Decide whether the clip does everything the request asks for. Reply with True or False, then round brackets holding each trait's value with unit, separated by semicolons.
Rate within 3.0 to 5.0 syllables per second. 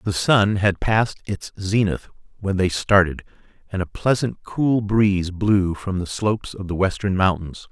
True (4.5 syllables/s)